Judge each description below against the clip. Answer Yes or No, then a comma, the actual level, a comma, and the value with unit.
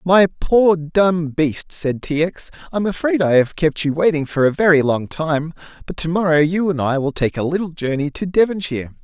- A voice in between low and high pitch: Yes, medium, 160 Hz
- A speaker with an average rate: No, fast, 210 wpm